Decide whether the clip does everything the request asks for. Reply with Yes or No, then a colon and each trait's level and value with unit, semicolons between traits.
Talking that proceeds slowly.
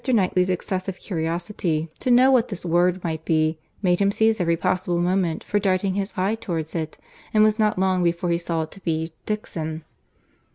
No: average, 195 wpm